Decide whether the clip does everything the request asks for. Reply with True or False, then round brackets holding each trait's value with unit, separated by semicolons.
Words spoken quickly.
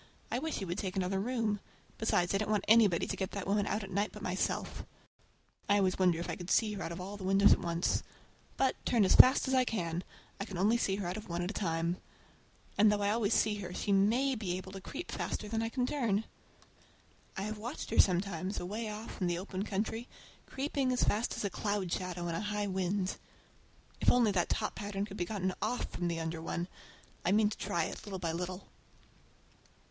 True (225 wpm)